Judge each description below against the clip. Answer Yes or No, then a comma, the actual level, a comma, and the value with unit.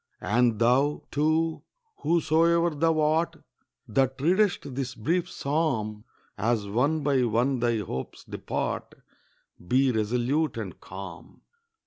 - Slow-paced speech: Yes, slow, 110 wpm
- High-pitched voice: No, low, 135 Hz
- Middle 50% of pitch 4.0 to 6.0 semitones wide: Yes, average, 5.2 semitones